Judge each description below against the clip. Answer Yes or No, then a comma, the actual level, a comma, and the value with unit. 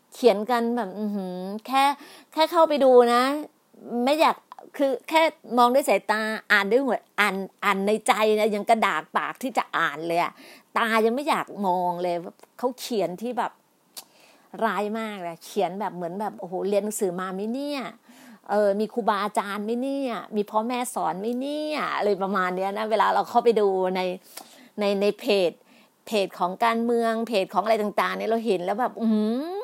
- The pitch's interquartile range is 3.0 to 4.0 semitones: Yes, average, 3.5 semitones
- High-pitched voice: Yes, high, 220 Hz